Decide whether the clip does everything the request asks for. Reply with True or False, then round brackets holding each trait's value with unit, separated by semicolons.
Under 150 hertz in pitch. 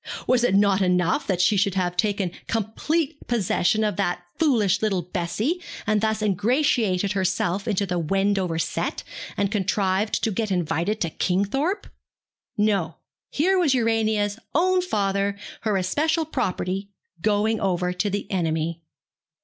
False (200 Hz)